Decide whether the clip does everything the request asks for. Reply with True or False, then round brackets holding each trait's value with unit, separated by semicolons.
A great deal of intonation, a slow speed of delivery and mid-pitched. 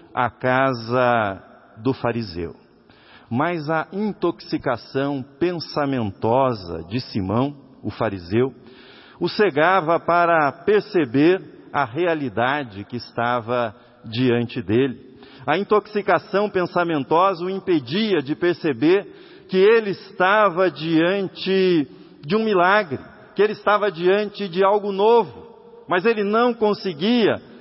True (7.7 semitones; 100 wpm; 165 Hz)